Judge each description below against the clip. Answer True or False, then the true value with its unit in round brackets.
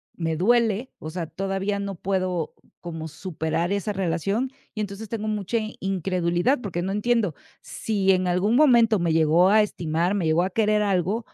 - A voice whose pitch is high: True (195 Hz)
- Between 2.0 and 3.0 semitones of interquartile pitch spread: False (3.5 semitones)